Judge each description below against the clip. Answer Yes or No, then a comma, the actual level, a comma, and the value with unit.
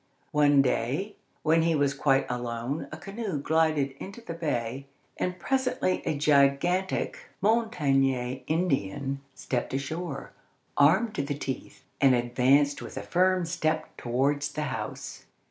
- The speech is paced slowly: Yes, slow, 130 wpm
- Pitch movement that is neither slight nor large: Yes, average, 4.3 semitones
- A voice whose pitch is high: No, medium, 145 Hz